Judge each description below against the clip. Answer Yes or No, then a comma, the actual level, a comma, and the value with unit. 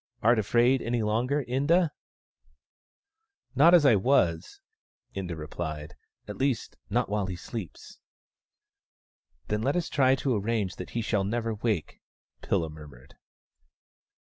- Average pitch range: No, wide, 6.5 semitones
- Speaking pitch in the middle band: No, low, 110 Hz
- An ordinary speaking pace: Yes, average, 145 wpm